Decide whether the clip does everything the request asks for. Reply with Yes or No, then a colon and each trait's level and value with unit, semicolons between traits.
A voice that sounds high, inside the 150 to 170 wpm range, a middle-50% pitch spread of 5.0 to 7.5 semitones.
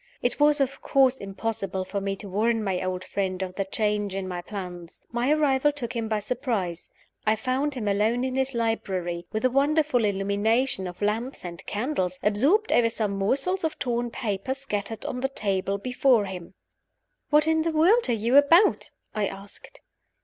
No: high, 225 Hz; average, 180 wpm; average, 5.3 semitones